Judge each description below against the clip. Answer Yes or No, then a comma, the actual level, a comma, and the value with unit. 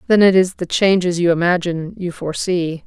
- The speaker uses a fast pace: No, average, 190 wpm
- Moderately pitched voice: Yes, medium, 180 Hz